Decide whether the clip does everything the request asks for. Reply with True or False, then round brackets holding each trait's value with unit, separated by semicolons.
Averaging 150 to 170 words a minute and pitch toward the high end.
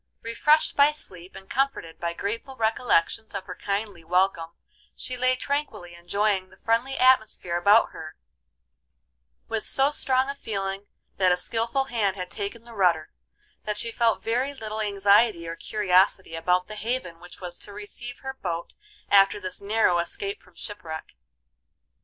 True (155 wpm; 205 Hz)